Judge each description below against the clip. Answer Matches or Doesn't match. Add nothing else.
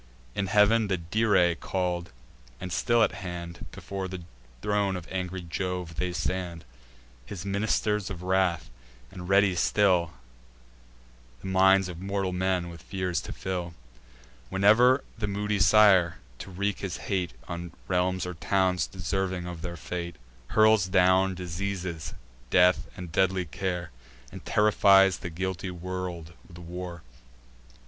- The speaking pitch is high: Doesn't match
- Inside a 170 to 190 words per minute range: Doesn't match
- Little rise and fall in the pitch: Matches